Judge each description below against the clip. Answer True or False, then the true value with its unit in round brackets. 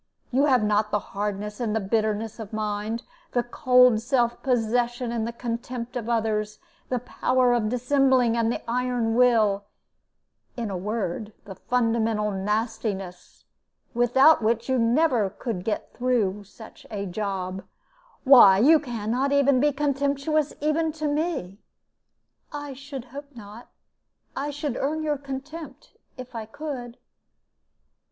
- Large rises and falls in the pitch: False (3.7 semitones)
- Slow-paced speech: True (130 wpm)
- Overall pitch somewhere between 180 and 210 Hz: False (235 Hz)